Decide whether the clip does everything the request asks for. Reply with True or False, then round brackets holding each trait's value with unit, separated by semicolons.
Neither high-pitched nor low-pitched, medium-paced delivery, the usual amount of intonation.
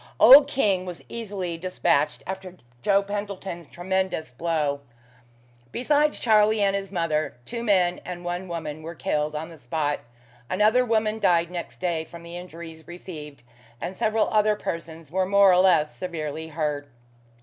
True (175 Hz; 150 wpm; 3.8 semitones)